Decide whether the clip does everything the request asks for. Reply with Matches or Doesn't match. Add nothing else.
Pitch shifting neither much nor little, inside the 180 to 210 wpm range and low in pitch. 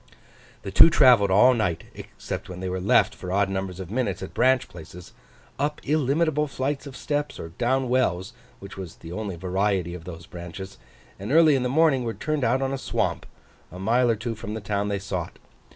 Doesn't match